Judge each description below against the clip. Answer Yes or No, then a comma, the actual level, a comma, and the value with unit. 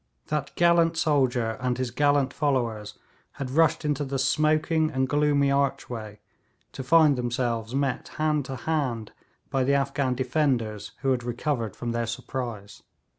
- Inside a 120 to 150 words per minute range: Yes, average, 145 wpm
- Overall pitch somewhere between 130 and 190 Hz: Yes, low, 135 Hz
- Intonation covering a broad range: No, average, 3.5 semitones